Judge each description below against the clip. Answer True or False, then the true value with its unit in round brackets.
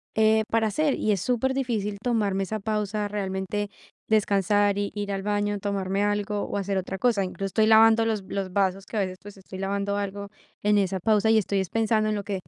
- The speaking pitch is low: False (205 Hz)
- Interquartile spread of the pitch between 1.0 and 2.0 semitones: True (1.7 semitones)